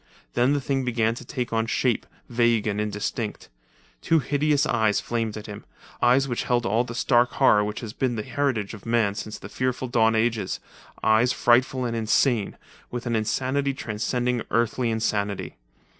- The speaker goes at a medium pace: Yes, average, 165 wpm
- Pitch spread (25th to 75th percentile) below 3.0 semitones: Yes, narrow, 2.5 semitones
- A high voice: No, low, 120 Hz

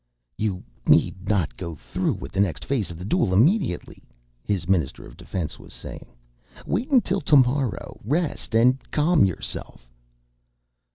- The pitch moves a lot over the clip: Yes, wide, 8.3 semitones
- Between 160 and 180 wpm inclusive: No, average, 145 wpm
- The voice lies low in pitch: Yes, low, 105 Hz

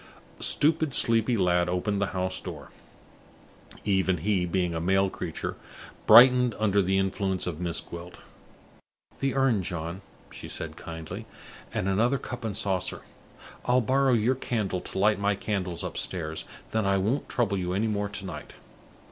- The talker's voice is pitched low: Yes, low, 100 Hz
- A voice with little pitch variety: No, average, 3.8 semitones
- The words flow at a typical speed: Yes, average, 160 wpm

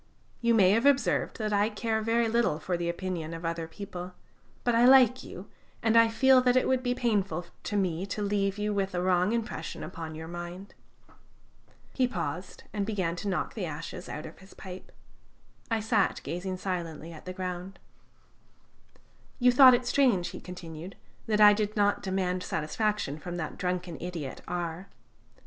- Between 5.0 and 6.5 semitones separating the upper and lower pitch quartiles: No, average, 4.1 semitones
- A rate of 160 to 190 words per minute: Yes, average, 175 wpm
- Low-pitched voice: No, high, 190 Hz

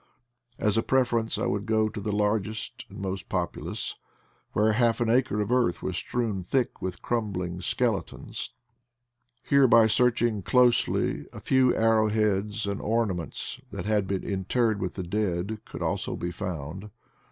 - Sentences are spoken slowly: No, average, 160 wpm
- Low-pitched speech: Yes, low, 105 Hz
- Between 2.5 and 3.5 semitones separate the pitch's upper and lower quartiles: Yes, average, 3.2 semitones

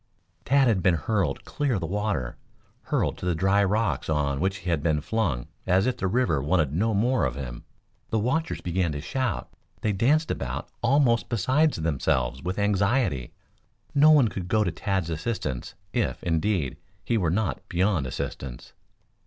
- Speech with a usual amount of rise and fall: No, wide, 6.4 semitones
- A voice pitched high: No, very low, 95 Hz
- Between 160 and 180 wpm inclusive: Yes, average, 170 wpm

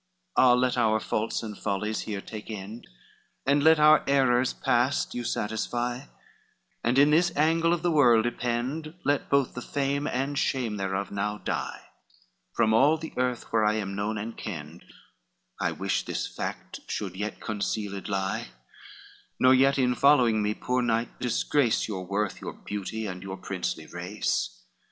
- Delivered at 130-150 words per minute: No, average, 165 wpm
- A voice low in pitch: Yes, low, 115 Hz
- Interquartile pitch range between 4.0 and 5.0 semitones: Yes, average, 4.6 semitones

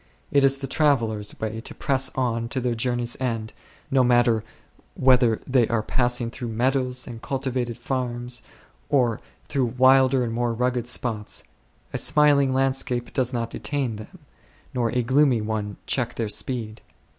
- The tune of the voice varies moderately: No, narrow, 2.2 semitones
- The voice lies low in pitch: Yes, low, 125 Hz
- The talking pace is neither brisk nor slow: Yes, average, 155 wpm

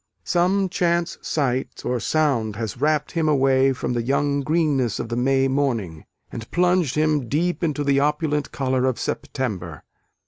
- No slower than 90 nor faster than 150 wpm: No, average, 160 wpm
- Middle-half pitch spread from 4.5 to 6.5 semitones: No, average, 3.7 semitones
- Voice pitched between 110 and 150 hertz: Yes, medium, 140 Hz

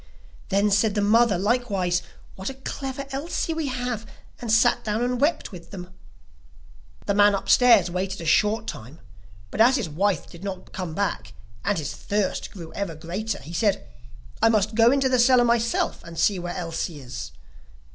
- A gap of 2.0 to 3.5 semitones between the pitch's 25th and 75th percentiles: No, average, 5.0 semitones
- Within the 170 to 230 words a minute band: Yes, average, 175 wpm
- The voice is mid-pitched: No, high, 205 Hz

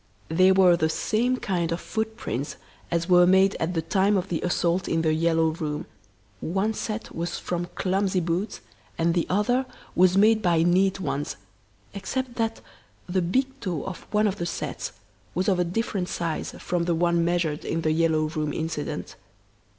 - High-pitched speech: No, medium, 175 Hz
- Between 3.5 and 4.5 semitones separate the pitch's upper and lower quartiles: No, average, 3.0 semitones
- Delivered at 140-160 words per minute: No, average, 175 wpm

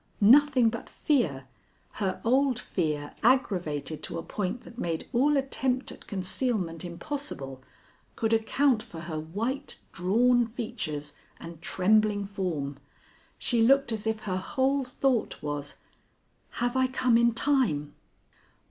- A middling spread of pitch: No, wide, 7.0 semitones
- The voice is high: Yes, high, 220 Hz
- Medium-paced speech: No, slow, 130 wpm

